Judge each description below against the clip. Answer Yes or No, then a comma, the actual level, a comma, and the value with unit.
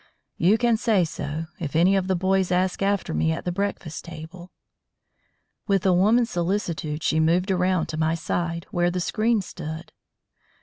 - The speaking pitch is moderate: Yes, medium, 180 Hz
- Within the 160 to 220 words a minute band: Yes, average, 170 wpm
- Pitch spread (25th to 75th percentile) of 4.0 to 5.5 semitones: No, average, 3.1 semitones